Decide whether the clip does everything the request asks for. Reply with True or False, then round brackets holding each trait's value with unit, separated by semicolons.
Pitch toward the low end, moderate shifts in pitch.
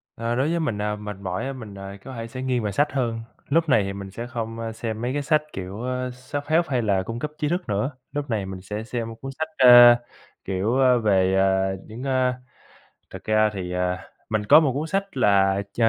True (115 Hz; 4.9 semitones)